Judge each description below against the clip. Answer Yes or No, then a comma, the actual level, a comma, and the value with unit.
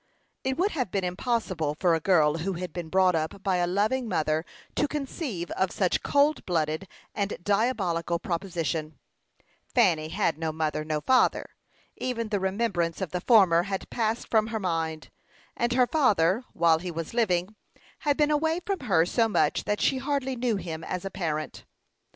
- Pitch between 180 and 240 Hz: Yes, high, 190 Hz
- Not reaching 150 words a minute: No, average, 180 wpm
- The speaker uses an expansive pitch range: Yes, wide, 6.0 semitones